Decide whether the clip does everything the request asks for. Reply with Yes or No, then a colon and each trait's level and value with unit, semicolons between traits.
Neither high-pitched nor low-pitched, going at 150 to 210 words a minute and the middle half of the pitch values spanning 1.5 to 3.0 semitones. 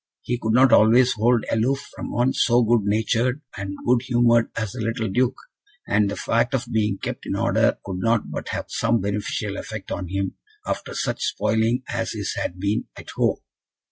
No: low, 115 Hz; average, 190 wpm; narrow, 2.6 semitones